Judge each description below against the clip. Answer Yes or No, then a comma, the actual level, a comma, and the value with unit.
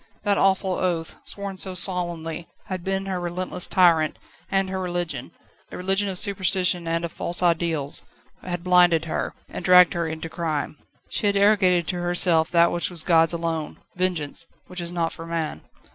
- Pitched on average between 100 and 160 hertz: No, medium, 175 Hz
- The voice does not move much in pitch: Yes, narrow, 2.0 semitones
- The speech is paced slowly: No, average, 175 wpm